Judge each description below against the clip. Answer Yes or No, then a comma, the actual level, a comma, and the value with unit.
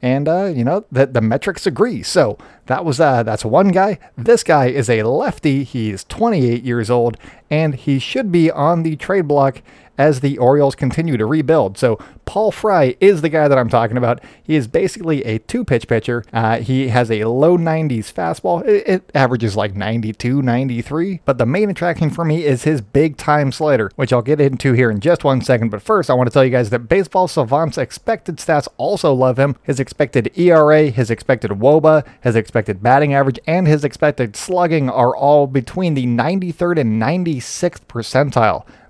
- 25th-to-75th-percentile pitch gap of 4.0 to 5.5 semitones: Yes, average, 4.9 semitones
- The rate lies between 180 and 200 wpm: Yes, average, 195 wpm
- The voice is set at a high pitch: No, medium, 140 Hz